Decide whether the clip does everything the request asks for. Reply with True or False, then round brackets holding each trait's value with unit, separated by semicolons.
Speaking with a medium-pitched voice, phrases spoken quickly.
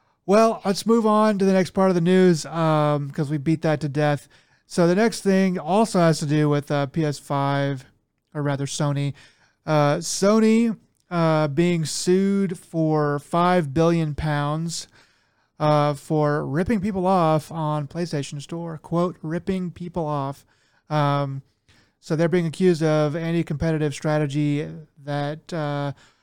False (155 Hz; 145 wpm)